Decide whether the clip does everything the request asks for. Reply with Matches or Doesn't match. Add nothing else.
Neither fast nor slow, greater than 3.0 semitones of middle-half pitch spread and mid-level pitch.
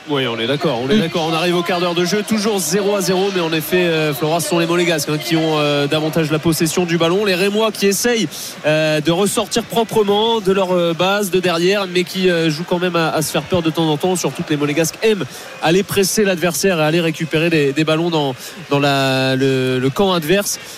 Doesn't match